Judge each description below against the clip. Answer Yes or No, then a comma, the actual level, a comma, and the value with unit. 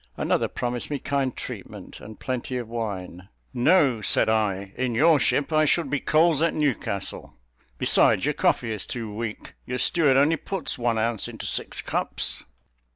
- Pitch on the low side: Yes, low, 125 Hz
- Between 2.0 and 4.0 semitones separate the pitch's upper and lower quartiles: No, average, 4.9 semitones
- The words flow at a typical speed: Yes, average, 165 wpm